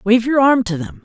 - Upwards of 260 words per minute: Yes, fast, 290 wpm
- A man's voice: Yes, male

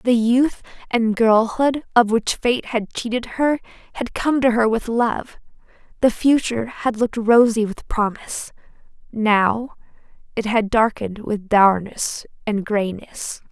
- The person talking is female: Yes, female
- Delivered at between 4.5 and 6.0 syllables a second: No, 4.1 syllables/s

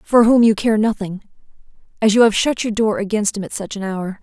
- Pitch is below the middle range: No, high, 210 Hz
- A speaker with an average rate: No, fast, 240 wpm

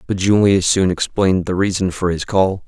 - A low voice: Yes, very low, 95 Hz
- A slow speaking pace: No, average, 200 wpm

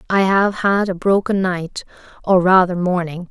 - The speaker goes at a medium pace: Yes, average, 165 wpm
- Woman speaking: Yes, female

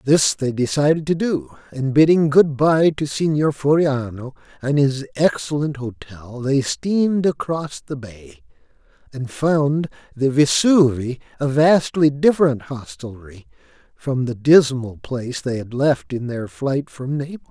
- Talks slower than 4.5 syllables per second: Yes, 4.2 syllables/s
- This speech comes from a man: Yes, male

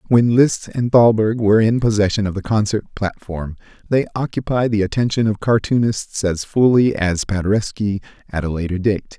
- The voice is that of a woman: No, male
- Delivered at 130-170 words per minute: Yes, average, 165 wpm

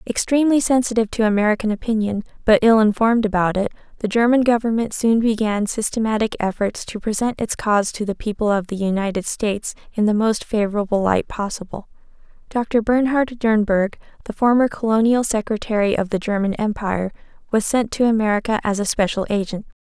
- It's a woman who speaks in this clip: Yes, female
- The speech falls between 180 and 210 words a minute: No, average, 160 wpm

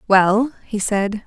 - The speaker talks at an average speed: Yes, average, 145 wpm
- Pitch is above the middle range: Yes, high, 210 Hz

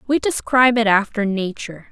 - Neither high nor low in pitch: No, high, 225 Hz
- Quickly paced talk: No, average, 155 wpm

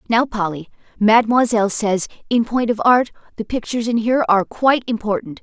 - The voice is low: No, high, 225 Hz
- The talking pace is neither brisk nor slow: Yes, average, 165 wpm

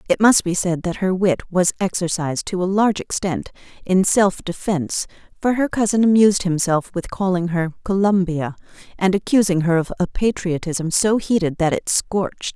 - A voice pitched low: No, medium, 185 Hz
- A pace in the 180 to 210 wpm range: No, average, 170 wpm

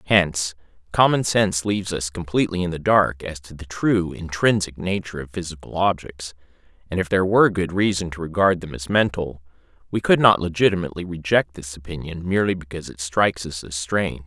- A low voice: Yes, very low, 90 Hz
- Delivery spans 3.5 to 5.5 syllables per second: No, 6.0 syllables/s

